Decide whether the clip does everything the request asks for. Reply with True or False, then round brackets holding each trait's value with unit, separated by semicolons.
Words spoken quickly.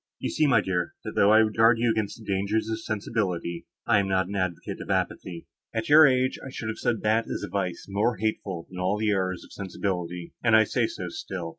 True (240 wpm)